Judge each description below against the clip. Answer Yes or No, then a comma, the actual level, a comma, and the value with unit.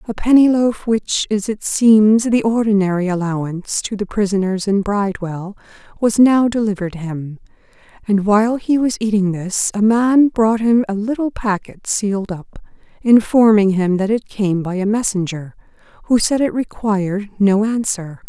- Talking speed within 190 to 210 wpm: No, average, 160 wpm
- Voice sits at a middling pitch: No, high, 210 Hz